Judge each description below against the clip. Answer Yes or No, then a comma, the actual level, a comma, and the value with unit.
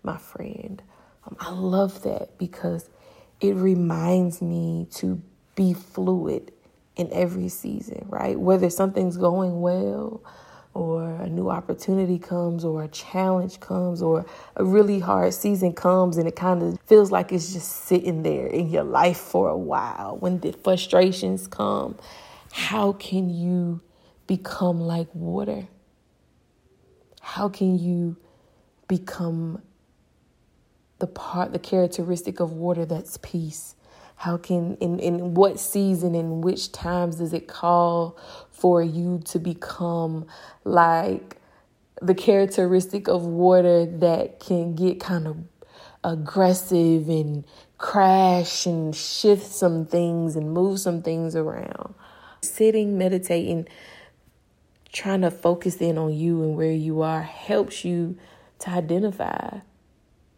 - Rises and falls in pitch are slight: Yes, narrow, 1.7 semitones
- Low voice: No, medium, 175 Hz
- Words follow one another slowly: Yes, slow, 125 wpm